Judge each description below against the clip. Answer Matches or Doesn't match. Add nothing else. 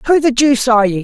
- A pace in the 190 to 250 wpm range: Doesn't match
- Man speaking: Doesn't match